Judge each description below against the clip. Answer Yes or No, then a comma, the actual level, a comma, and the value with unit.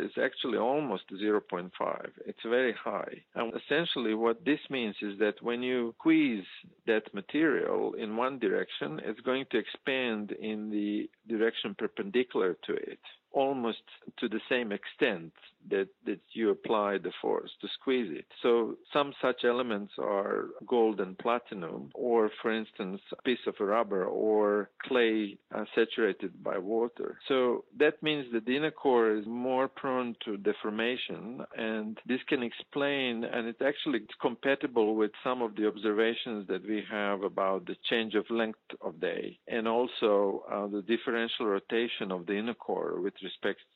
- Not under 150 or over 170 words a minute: Yes, average, 160 wpm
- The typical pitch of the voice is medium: No, low, 115 Hz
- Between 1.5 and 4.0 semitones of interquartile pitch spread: Yes, average, 3.7 semitones